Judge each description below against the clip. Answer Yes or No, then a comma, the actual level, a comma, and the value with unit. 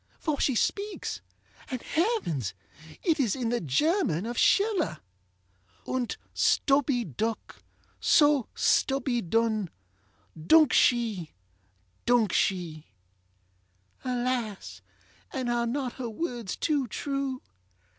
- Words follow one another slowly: Yes, slow, 100 wpm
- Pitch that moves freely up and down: No, average, 4.6 semitones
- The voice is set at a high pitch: Yes, high, 245 Hz